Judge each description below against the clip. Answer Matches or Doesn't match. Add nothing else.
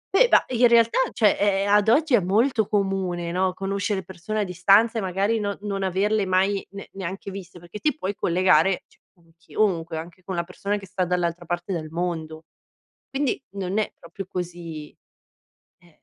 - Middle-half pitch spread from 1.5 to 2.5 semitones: Doesn't match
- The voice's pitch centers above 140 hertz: Matches